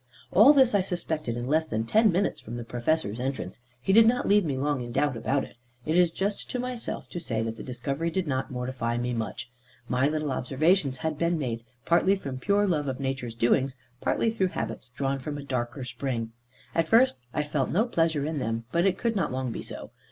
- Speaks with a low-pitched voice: No, medium, 145 Hz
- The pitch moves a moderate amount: No, wide, 6.1 semitones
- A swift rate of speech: Yes, fast, 225 wpm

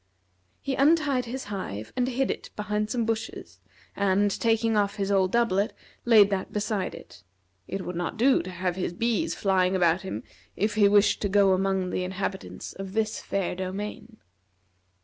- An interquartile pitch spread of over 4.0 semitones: No, average, 3.1 semitones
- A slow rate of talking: No, average, 170 wpm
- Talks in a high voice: Yes, high, 200 Hz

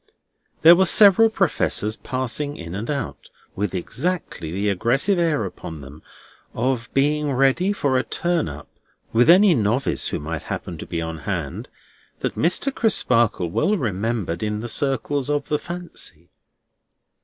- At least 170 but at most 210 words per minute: No, average, 150 wpm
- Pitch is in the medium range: No, low, 130 Hz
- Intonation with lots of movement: Yes, wide, 8.6 semitones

